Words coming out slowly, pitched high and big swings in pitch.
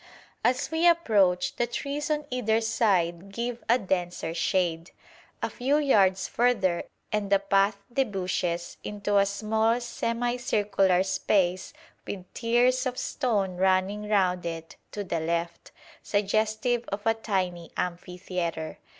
No: slow, 125 wpm; high, 200 Hz; average, 4.5 semitones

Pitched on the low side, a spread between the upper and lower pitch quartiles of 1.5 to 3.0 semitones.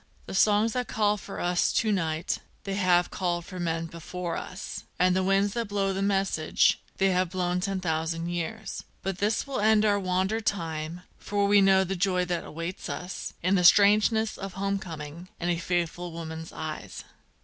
No: medium, 185 Hz; average, 2.7 semitones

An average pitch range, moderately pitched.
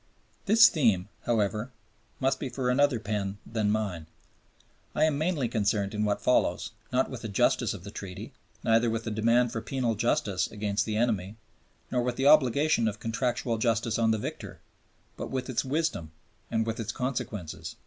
No: average, 3.4 semitones; low, 115 Hz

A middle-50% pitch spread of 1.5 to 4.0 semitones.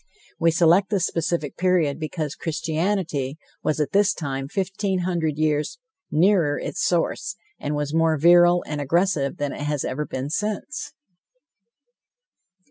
Yes: average, 3.7 semitones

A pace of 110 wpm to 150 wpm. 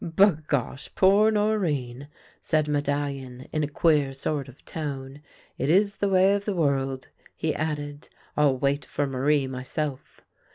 No: average, 160 wpm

